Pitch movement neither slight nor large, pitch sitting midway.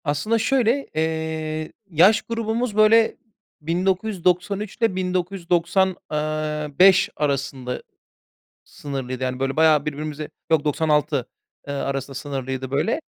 Yes: average, 4.9 semitones; medium, 160 Hz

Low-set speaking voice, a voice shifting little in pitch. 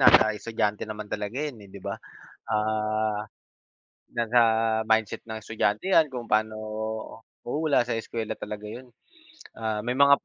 Yes: low, 110 Hz; narrow, 1.8 semitones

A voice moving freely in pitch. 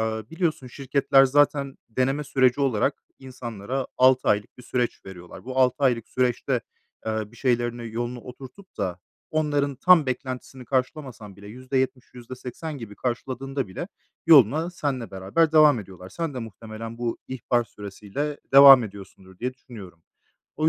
No: average, 3.5 semitones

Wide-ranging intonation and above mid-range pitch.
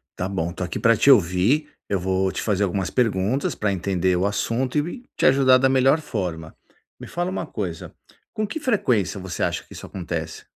No: wide, 6.4 semitones; low, 100 Hz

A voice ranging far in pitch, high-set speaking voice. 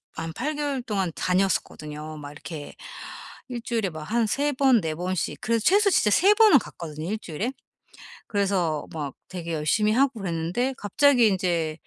Yes: wide, 7.4 semitones; high, 195 Hz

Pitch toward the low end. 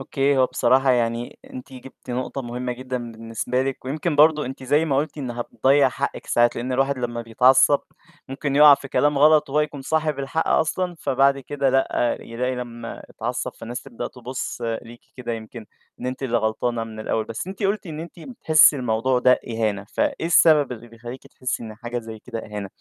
Yes: low, 130 Hz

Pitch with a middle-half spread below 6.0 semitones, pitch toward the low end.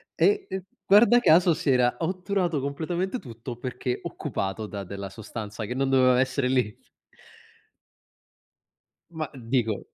No: wide, 6.9 semitones; low, 130 Hz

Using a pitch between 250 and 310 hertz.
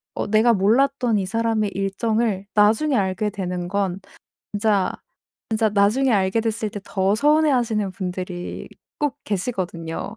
No: high, 210 Hz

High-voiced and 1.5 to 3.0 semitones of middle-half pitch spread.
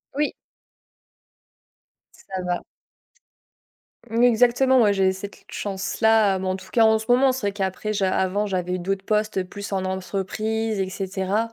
Yes: high, 200 Hz; average, 2.7 semitones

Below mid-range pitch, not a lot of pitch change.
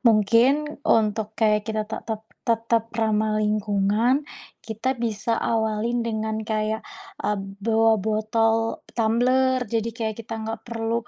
No: high, 225 Hz; narrow, 1.3 semitones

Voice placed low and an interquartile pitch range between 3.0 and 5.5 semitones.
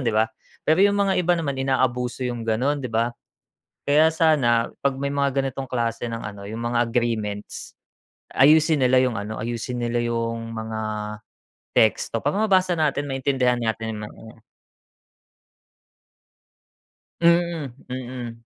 Yes: low, 125 Hz; average, 3.8 semitones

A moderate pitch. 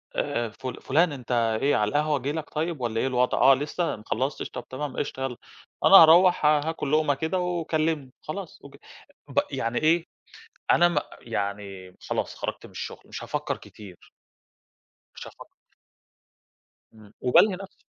Yes: medium, 145 Hz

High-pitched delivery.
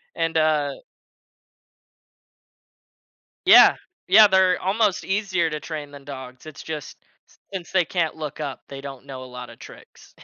No: medium, 155 Hz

